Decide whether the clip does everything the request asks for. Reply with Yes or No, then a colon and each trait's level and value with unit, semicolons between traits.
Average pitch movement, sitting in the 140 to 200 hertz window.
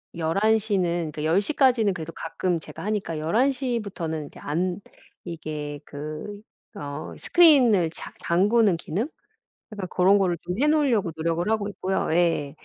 Yes: average, 4.9 semitones; medium, 185 Hz